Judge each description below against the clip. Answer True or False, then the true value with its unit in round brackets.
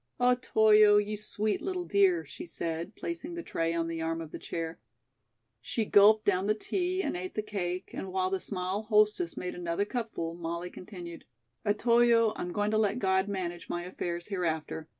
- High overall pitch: True (200 Hz)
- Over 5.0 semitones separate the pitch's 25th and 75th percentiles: False (4.0 semitones)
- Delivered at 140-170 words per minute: False (180 wpm)